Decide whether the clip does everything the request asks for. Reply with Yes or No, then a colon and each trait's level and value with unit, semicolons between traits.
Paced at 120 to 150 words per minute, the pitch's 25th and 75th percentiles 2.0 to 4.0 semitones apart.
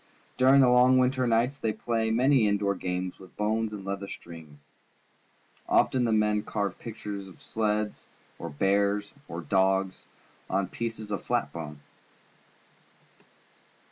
Yes: average, 140 wpm; average, 3.0 semitones